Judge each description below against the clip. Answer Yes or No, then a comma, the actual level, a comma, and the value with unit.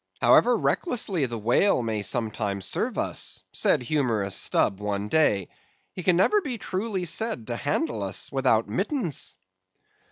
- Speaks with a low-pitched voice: Yes, low, 125 Hz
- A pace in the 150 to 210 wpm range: No, average, 140 wpm